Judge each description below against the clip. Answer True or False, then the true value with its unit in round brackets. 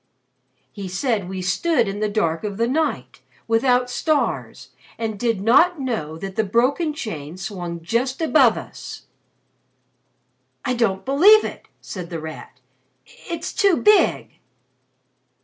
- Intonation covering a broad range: True (6.5 semitones)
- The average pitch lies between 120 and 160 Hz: False (225 Hz)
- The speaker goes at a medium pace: False (130 wpm)